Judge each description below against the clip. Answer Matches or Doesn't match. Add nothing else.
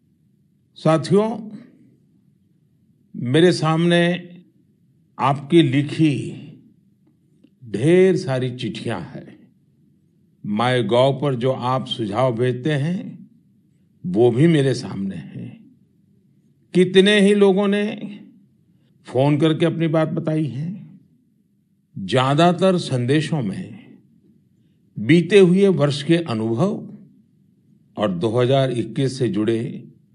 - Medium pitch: Matches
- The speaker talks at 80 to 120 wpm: Matches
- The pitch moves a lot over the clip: Matches